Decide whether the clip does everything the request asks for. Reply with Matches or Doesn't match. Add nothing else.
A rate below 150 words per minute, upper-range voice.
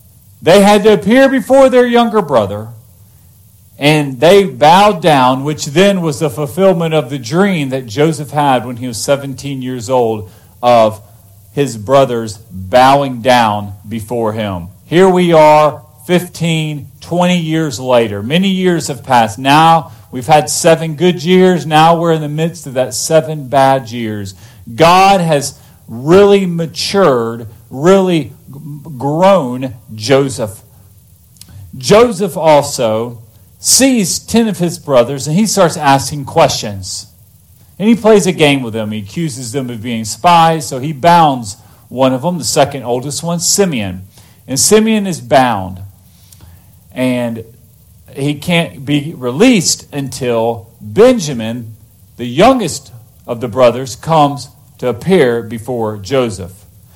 Doesn't match